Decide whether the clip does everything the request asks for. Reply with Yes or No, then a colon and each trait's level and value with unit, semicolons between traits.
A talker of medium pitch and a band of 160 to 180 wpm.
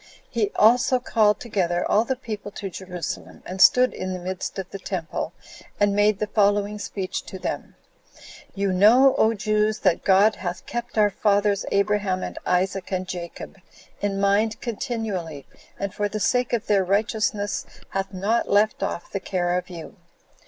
No: high, 200 Hz; average, 165 wpm